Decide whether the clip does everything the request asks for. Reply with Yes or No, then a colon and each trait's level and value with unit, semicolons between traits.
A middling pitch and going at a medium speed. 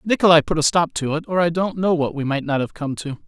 No: medium, 160 Hz; fast, 310 wpm